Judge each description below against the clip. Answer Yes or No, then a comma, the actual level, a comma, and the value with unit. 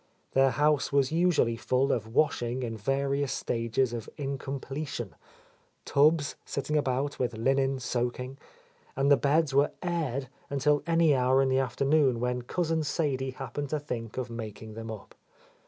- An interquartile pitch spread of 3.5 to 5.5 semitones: No, average, 2.7 semitones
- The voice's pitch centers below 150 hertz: Yes, low, 135 Hz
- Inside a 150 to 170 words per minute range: Yes, average, 160 wpm